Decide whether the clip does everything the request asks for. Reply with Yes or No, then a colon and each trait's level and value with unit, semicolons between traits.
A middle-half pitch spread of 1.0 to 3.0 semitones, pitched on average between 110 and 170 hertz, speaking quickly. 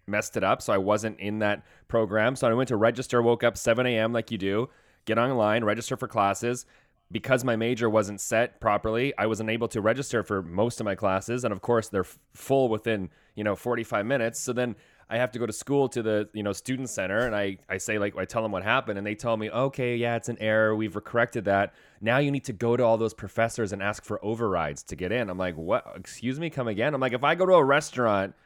Yes: narrow, 2.6 semitones; low, 115 Hz; fast, 255 wpm